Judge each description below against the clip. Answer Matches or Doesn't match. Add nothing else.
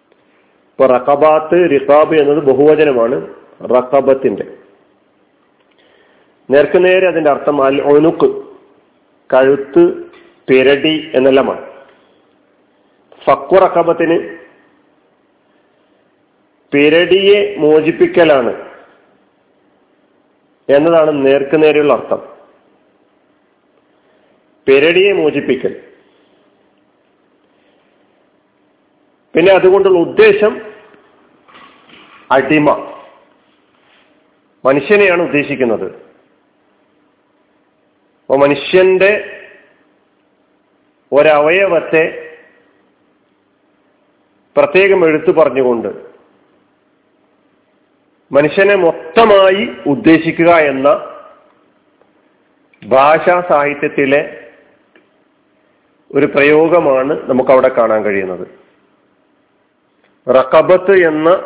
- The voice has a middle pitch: Matches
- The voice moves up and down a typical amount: Doesn't match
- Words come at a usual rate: Doesn't match